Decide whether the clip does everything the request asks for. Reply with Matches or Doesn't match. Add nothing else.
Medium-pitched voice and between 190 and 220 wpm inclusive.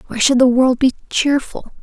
Doesn't match